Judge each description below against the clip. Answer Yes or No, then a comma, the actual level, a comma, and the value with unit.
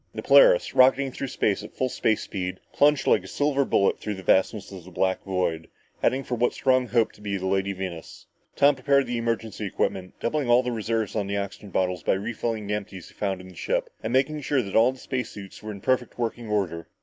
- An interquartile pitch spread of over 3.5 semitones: Yes, average, 4.9 semitones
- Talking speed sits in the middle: No, fast, 230 wpm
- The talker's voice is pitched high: No, low, 110 Hz